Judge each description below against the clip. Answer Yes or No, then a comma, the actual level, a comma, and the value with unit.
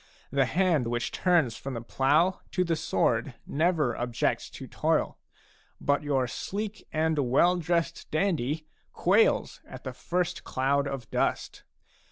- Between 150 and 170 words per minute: No, average, 140 wpm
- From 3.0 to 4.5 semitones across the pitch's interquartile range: No, average, 4.9 semitones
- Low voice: No, medium, 155 Hz